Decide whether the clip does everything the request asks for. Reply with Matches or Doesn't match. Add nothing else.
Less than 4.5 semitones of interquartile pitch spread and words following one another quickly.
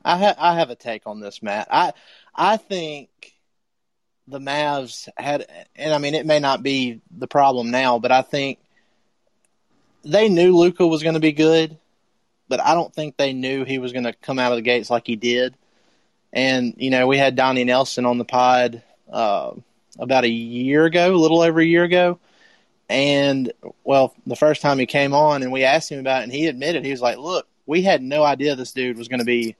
Matches